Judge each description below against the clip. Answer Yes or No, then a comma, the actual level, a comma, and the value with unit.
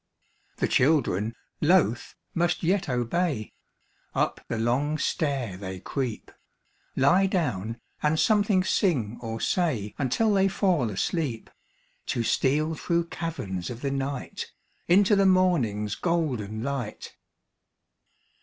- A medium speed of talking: No, slow, 115 wpm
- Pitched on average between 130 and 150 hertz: Yes, medium, 140 Hz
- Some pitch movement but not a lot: No, wide, 7.3 semitones